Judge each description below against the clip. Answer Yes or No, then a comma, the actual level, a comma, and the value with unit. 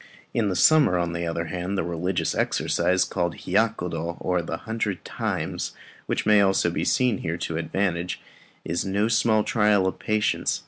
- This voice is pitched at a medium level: No, very low, 95 Hz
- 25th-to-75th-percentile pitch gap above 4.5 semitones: No, average, 3.6 semitones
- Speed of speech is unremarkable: Yes, average, 165 wpm